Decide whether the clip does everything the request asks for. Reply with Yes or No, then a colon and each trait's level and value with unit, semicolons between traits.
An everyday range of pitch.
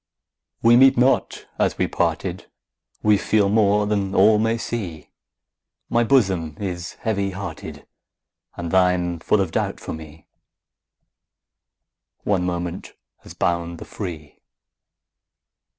Yes: average, 3.6 semitones